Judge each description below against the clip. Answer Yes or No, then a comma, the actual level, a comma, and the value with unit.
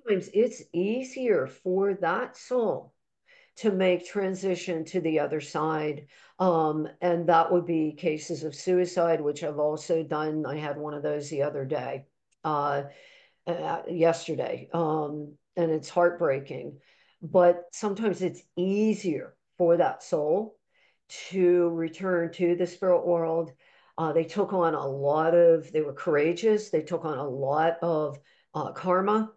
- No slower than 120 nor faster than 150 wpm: Yes, average, 145 wpm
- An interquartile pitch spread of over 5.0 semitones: No, average, 3.1 semitones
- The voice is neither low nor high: Yes, medium, 170 Hz